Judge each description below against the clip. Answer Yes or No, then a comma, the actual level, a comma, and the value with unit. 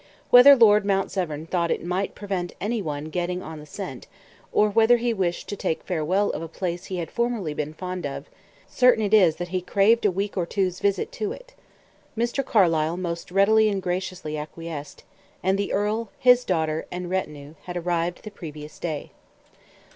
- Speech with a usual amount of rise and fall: Yes, average, 3.9 semitones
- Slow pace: No, average, 185 wpm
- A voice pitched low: No, medium, 185 Hz